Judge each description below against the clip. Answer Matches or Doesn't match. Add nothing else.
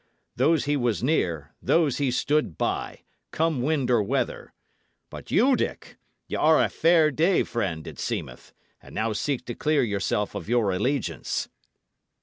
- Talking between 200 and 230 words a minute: Doesn't match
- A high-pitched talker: Doesn't match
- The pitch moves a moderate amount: Doesn't match